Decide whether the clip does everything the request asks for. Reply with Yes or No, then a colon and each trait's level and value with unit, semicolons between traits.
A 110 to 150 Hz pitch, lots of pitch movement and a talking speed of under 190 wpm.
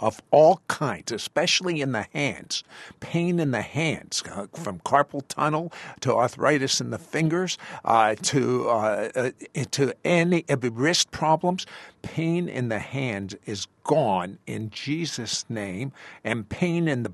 Yes: medium, 140 Hz; wide, 6.6 semitones; slow, 135 wpm